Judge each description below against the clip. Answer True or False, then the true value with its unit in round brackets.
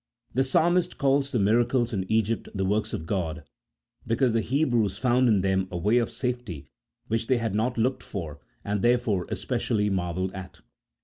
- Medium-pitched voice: False (110 Hz)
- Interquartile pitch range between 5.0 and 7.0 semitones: False (4.3 semitones)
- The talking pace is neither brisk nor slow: True (175 wpm)